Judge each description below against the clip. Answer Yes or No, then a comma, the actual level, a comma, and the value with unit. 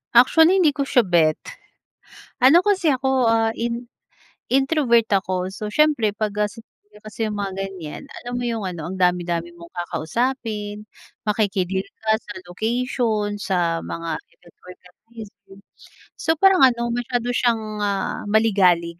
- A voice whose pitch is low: No, high, 215 Hz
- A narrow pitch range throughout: No, average, 4.5 semitones